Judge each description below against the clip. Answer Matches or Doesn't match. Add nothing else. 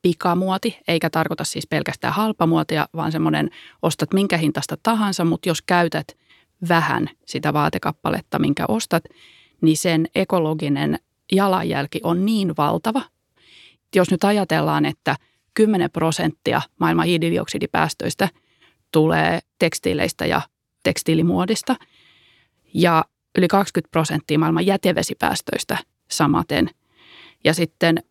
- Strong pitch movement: Doesn't match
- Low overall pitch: Doesn't match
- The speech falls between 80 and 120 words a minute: Matches